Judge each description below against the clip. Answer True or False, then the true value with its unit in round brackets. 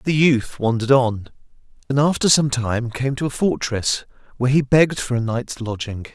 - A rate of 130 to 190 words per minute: True (185 wpm)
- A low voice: True (125 Hz)